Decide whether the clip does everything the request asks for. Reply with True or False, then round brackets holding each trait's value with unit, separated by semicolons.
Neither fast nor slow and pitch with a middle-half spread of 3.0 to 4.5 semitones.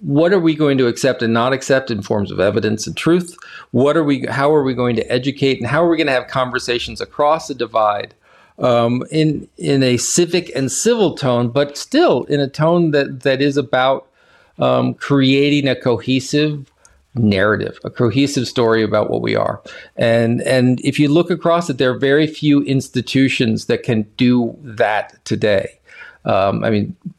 True (185 wpm; 3.4 semitones)